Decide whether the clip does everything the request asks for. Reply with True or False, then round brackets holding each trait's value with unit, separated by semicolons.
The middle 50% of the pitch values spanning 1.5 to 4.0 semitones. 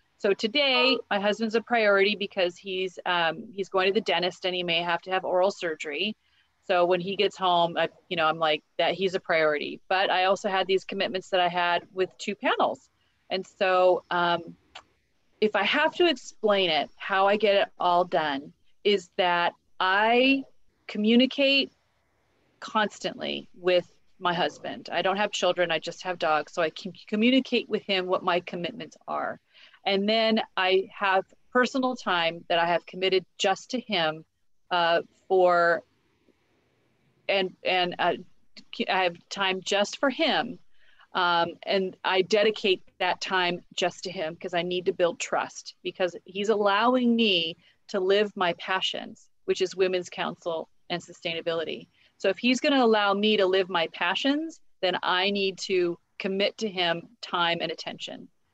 True (3.0 semitones)